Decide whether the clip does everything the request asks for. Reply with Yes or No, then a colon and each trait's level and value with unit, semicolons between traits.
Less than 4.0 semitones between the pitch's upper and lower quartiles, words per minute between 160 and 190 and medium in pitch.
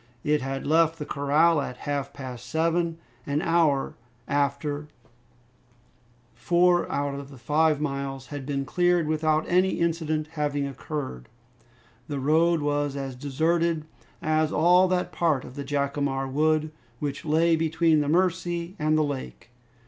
No: average, 2.8 semitones; average, 140 wpm; medium, 150 Hz